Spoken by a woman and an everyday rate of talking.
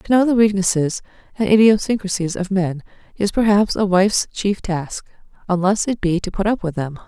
Yes: female; average, 185 wpm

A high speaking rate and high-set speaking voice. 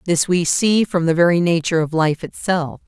No: fast, 210 wpm; medium, 170 Hz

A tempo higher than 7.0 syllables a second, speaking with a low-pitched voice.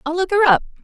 No: 7.3 syllables/s; very high, 350 Hz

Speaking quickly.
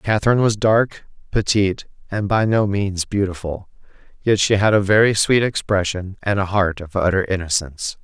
No: average, 165 wpm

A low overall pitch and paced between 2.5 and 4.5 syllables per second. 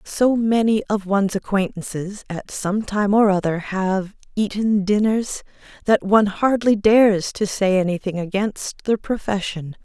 No: high, 200 Hz; 4.3 syllables/s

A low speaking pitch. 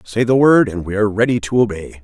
Yes: low, 110 Hz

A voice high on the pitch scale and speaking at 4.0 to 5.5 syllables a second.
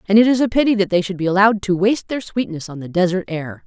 No: high, 195 Hz; 6.9 syllables/s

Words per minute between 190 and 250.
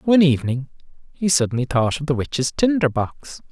No: average, 170 wpm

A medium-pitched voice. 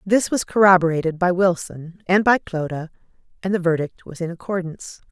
Yes: medium, 180 Hz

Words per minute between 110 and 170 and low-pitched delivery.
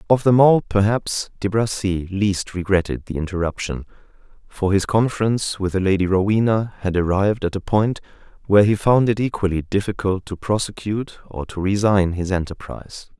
Yes: average, 160 wpm; low, 100 Hz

